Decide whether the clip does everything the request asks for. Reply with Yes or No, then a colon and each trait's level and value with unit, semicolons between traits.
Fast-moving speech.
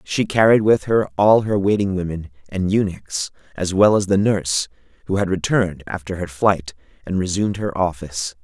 No: average, 180 wpm